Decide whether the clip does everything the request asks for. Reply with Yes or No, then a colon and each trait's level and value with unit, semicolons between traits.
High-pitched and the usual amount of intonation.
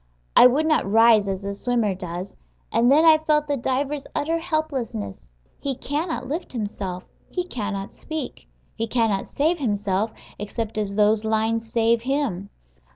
No: high, 230 Hz; wide, 6.0 semitones